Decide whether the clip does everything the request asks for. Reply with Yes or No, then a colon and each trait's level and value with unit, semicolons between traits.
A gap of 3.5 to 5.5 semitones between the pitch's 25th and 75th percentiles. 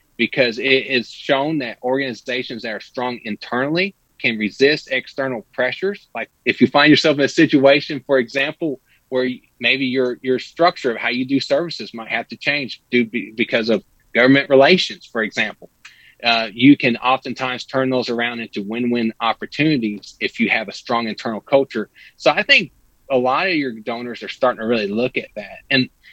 No: narrow, 2.6 semitones